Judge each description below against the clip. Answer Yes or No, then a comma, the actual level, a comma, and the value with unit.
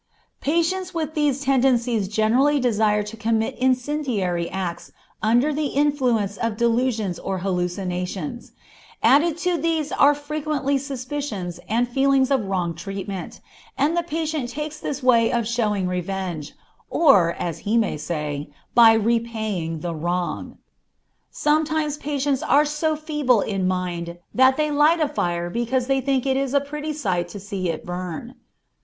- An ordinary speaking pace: Yes, average, 150 wpm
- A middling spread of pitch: No, wide, 7.2 semitones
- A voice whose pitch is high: Yes, high, 240 Hz